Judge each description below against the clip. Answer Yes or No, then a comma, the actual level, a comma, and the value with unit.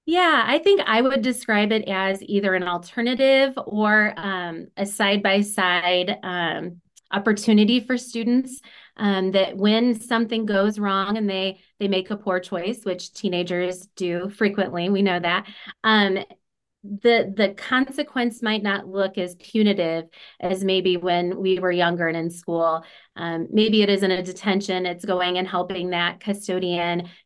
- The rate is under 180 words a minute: Yes, average, 155 wpm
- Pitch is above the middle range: Yes, high, 195 Hz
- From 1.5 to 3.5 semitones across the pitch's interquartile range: Yes, average, 3.1 semitones